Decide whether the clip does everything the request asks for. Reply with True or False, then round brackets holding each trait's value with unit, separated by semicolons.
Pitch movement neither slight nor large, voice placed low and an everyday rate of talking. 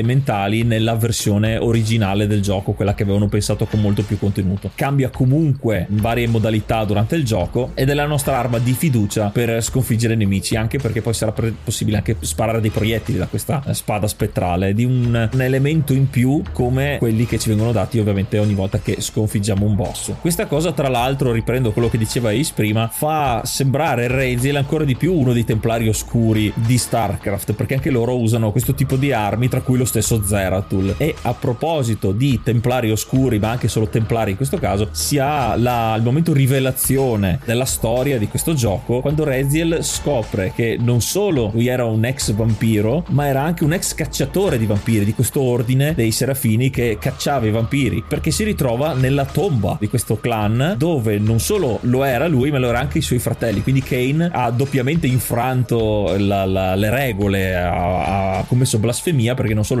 False (3.6 semitones; 115 Hz; 190 wpm)